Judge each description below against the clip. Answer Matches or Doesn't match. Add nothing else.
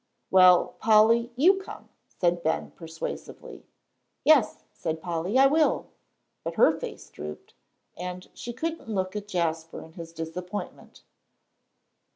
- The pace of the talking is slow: Matches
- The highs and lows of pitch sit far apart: Matches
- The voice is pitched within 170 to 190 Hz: Matches